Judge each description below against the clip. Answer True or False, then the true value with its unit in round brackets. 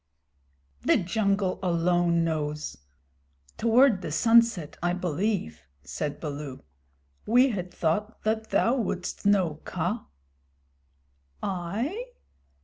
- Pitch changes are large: False (5.0 semitones)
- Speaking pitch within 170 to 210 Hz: True (185 Hz)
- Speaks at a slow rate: True (95 wpm)